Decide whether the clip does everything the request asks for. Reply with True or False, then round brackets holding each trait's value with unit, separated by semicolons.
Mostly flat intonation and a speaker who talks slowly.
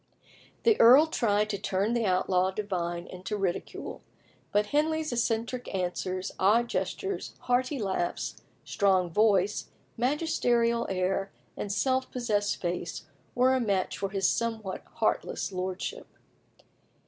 False (4.3 semitones; 120 wpm)